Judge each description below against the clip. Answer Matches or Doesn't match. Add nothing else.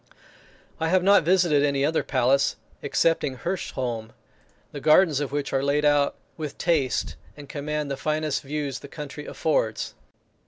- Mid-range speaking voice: Matches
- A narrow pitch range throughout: Matches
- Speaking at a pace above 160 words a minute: Doesn't match